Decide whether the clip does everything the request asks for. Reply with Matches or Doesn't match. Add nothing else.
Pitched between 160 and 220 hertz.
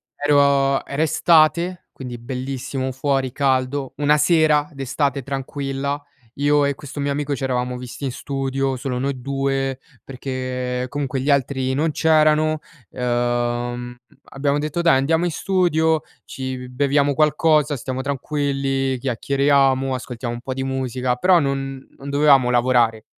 Doesn't match